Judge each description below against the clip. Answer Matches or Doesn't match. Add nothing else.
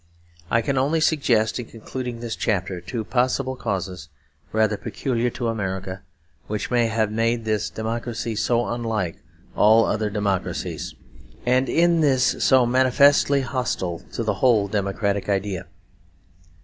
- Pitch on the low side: Matches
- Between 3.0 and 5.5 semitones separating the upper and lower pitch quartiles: Matches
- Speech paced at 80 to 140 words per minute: Matches